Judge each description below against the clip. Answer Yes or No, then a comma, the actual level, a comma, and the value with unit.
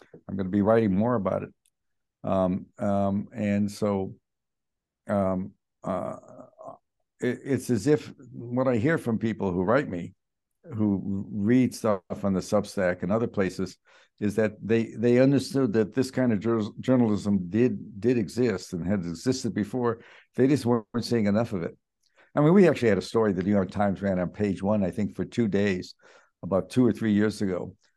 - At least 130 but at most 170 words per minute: No, average, 185 wpm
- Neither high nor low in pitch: No, low, 105 Hz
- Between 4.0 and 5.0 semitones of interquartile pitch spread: No, average, 3.5 semitones